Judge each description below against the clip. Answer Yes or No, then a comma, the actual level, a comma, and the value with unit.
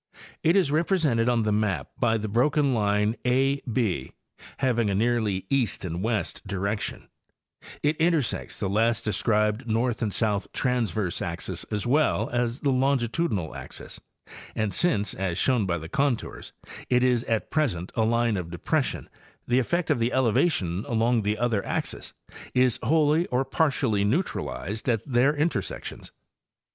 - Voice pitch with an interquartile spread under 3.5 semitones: No, average, 4.3 semitones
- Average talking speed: Yes, average, 155 wpm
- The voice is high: No, low, 115 Hz